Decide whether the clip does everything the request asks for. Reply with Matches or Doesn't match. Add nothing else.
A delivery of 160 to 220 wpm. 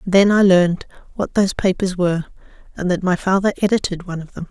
Matches